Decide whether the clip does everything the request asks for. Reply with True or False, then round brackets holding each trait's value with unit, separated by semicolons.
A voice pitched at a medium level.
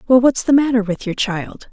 False (230 Hz)